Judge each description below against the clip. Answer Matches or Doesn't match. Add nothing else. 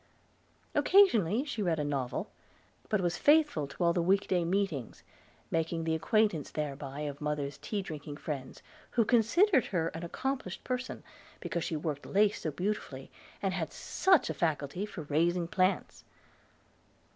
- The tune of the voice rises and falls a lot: Matches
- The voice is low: Doesn't match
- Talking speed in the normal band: Matches